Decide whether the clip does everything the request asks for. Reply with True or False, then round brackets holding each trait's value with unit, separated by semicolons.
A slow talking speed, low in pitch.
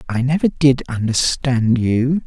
True (130 wpm; 130 Hz)